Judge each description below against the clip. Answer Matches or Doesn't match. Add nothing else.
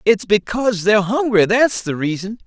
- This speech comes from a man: Matches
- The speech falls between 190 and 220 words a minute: Doesn't match